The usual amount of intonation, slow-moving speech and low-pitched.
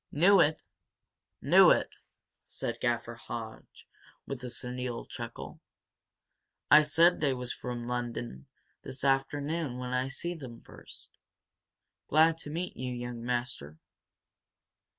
Yes: average, 3.6 semitones; slow, 120 wpm; low, 125 Hz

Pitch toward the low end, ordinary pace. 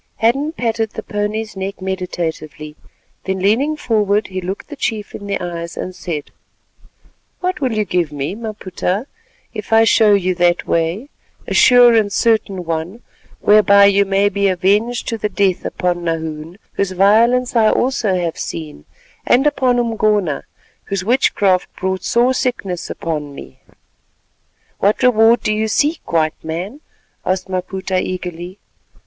No: high, 200 Hz; average, 145 wpm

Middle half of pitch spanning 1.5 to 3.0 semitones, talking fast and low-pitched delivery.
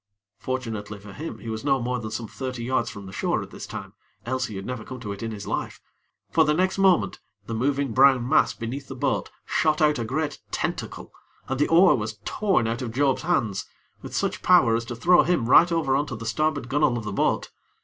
No: average, 4.7 semitones; fast, 230 wpm; low, 130 Hz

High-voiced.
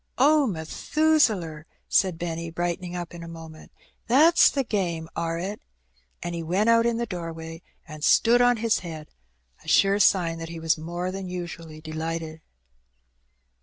No: medium, 170 Hz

